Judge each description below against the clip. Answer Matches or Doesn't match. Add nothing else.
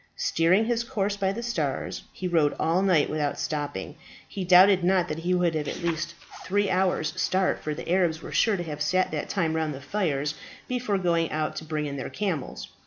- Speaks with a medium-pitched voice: Matches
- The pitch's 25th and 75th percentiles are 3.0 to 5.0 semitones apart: Matches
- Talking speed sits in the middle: Doesn't match